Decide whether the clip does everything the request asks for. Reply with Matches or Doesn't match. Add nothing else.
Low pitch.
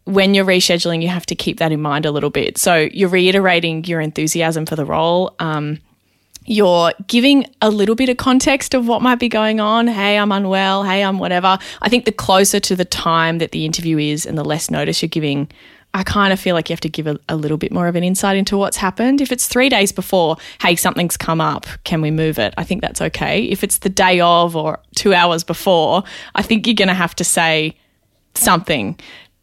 Doesn't match